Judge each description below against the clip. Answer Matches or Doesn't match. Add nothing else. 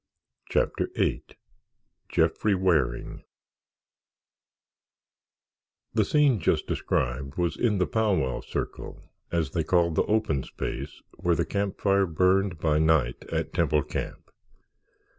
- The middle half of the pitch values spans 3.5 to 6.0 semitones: Matches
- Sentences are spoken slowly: Matches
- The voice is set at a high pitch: Doesn't match